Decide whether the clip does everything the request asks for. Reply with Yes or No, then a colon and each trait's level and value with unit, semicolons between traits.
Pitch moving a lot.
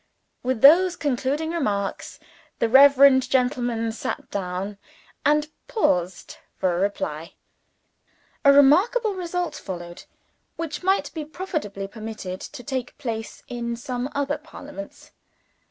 Yes: wide, 6.3 semitones